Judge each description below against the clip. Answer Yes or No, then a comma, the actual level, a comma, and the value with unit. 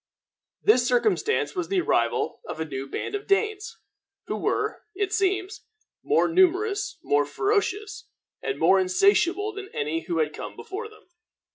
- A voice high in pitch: Yes, very high, 385 Hz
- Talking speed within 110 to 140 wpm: No, average, 150 wpm